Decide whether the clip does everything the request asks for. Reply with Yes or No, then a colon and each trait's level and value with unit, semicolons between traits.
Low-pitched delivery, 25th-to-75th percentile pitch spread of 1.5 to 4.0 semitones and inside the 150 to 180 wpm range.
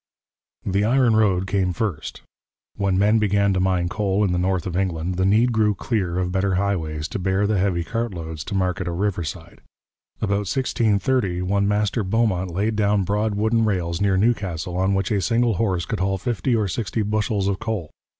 No: low, 100 Hz; average, 2.7 semitones; average, 190 wpm